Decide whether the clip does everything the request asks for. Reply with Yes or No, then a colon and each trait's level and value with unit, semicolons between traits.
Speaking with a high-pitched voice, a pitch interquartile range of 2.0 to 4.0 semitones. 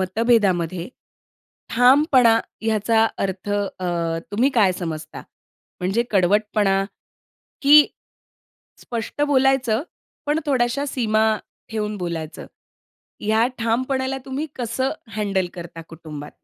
No: high, 220 Hz; average, 5.2 semitones